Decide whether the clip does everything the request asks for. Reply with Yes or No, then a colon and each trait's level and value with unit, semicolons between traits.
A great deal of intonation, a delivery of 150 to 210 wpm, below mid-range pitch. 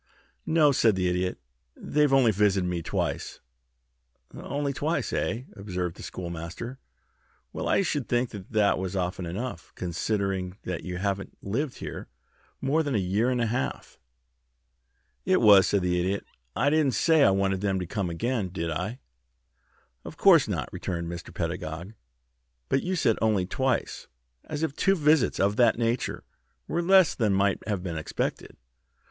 Yes: wide, 6.2 semitones; average, 160 wpm; low, 100 Hz